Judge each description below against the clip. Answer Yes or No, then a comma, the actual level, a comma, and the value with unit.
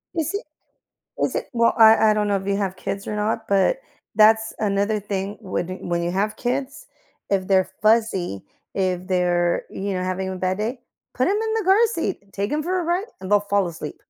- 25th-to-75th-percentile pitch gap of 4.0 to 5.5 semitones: No, average, 3.6 semitones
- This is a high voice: Yes, high, 205 Hz